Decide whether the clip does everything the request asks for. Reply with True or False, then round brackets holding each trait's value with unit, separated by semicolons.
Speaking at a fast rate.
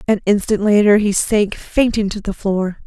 False (190 wpm)